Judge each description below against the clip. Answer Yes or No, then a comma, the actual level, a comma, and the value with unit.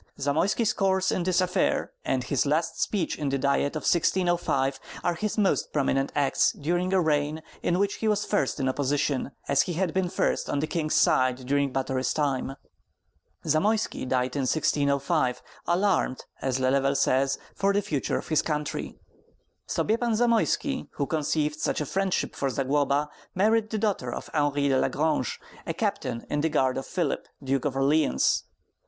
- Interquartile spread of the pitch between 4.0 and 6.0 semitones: Yes, average, 5.1 semitones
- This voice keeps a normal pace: Yes, average, 170 wpm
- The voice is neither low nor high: Yes, medium, 150 Hz